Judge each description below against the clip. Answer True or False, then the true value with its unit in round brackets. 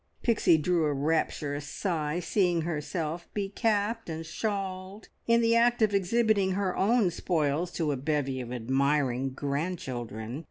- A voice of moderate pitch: True (170 Hz)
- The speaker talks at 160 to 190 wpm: False (145 wpm)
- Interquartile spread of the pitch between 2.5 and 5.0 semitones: False (5.6 semitones)